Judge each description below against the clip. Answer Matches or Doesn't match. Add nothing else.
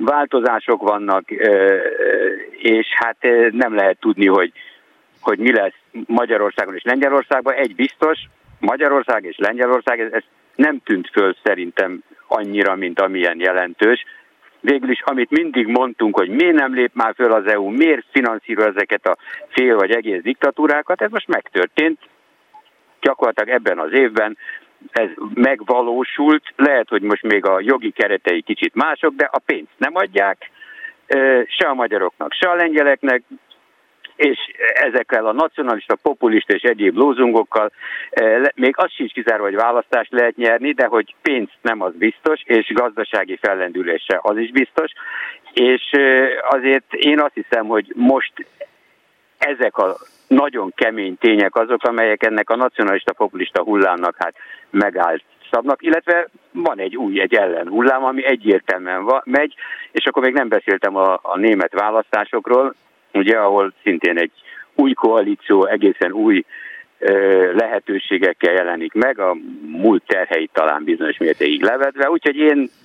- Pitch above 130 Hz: Matches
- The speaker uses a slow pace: Doesn't match